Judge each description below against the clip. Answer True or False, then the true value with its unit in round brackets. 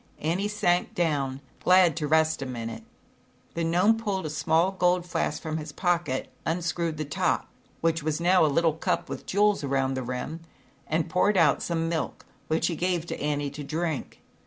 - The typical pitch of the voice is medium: True (165 Hz)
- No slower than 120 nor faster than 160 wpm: False (180 wpm)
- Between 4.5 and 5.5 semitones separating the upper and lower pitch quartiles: False (3.0 semitones)